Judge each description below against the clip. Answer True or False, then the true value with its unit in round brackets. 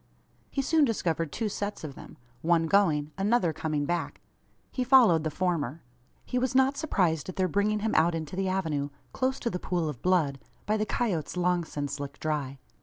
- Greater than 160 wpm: True (190 wpm)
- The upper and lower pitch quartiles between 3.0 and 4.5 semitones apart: False (5.4 semitones)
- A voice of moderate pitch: True (180 Hz)